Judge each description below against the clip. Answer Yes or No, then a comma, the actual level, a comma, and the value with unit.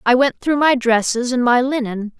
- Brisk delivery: Yes, fast, 220 wpm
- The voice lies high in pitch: Yes, very high, 250 Hz